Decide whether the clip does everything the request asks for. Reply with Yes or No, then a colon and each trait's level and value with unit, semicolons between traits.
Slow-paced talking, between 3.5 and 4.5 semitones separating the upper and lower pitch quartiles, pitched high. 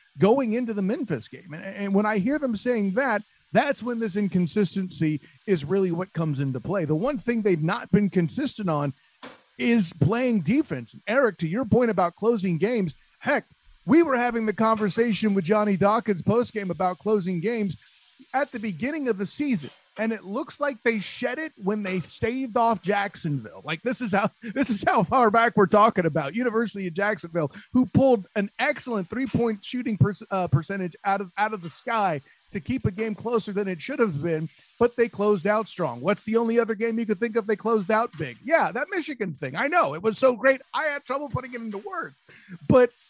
No: fast, 205 wpm; average, 4.0 semitones; high, 215 Hz